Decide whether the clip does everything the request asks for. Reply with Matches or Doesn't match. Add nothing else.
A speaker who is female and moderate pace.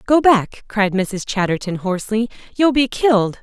Matches